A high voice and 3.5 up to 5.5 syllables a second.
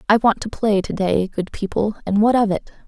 Yes: high, 210 Hz; 5.2 syllables/s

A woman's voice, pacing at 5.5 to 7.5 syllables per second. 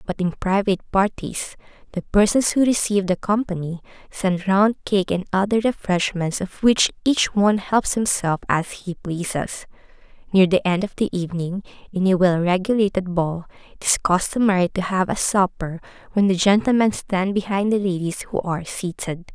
No: female; 5.0 syllables/s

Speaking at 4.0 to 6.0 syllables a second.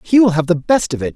No: 6.4 syllables/s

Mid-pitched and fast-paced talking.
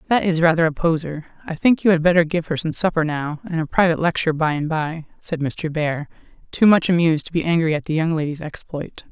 Yes: medium, 165 Hz; fast, 235 wpm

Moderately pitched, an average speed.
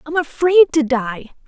No: very high, 295 Hz; average, 160 wpm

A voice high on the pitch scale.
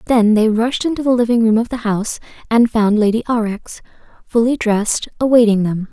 Yes: high, 225 Hz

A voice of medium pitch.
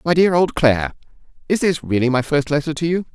Yes: medium, 150 Hz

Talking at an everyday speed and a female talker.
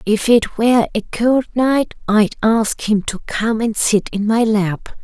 Yes: average, 190 wpm; female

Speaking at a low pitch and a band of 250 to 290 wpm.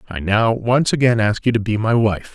Yes: low, 110 Hz; fast, 255 wpm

